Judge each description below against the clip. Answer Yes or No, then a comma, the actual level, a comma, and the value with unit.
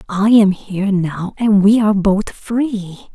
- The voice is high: Yes, high, 205 Hz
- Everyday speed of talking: Yes, average, 170 wpm